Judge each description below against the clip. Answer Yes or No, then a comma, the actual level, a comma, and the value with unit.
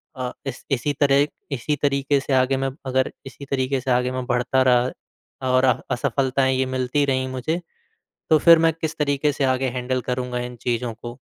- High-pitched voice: No, low, 130 Hz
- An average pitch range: No, narrow, 1.8 semitones